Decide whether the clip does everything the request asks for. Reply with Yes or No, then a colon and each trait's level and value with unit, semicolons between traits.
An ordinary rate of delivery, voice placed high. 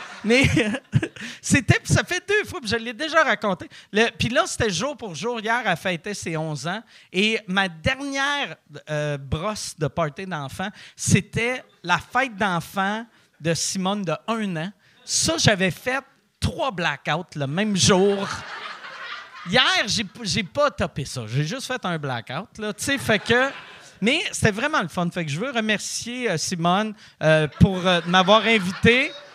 Yes: average, 165 wpm; high, 200 Hz